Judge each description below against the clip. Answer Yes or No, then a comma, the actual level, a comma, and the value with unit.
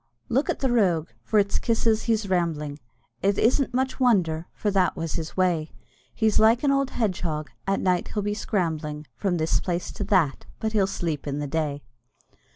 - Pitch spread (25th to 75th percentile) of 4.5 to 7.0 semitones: Yes, wide, 5.4 semitones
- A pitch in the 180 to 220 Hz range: Yes, medium, 185 Hz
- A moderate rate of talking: Yes, average, 190 wpm